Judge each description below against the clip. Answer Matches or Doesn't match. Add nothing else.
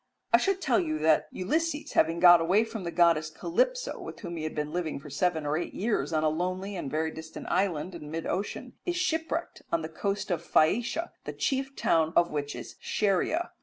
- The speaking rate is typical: Doesn't match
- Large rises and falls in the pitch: Matches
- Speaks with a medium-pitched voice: Matches